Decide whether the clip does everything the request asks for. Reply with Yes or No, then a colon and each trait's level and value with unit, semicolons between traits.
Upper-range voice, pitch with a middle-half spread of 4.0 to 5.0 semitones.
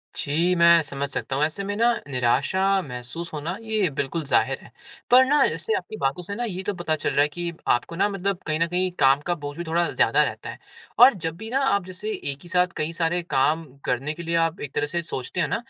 No: medium, 170 Hz; average, 4.4 semitones